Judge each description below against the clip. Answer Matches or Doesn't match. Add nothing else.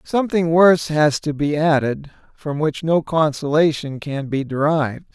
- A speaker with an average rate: Matches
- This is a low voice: Doesn't match